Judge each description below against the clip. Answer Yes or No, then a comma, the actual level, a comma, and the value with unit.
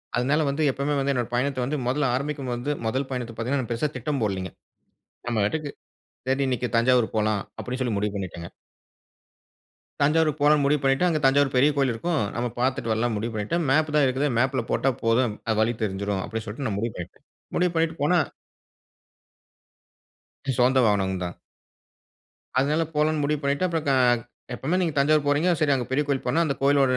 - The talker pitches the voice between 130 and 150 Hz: Yes, low, 135 Hz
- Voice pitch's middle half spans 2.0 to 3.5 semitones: No, average, 4.1 semitones